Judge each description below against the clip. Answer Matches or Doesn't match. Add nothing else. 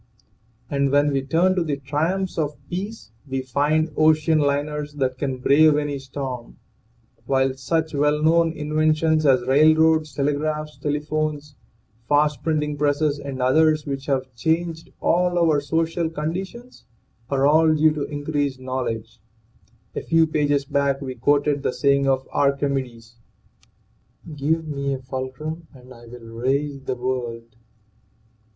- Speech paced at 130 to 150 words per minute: Matches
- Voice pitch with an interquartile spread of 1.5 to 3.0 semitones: Matches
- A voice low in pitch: Doesn't match